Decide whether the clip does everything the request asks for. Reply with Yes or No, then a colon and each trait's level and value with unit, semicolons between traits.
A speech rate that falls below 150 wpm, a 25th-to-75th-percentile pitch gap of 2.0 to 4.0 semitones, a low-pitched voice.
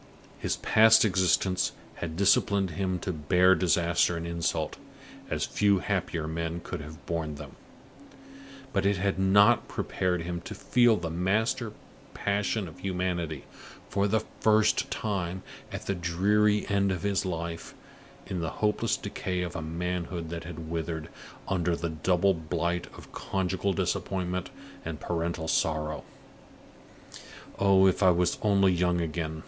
Yes: average, 140 wpm; average, 2.8 semitones; very low, 90 Hz